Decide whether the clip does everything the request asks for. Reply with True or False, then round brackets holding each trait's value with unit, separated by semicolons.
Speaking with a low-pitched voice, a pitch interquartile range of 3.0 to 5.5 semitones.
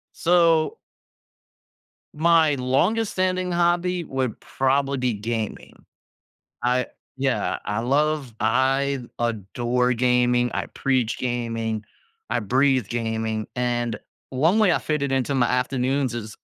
True (130 Hz; 3.9 semitones)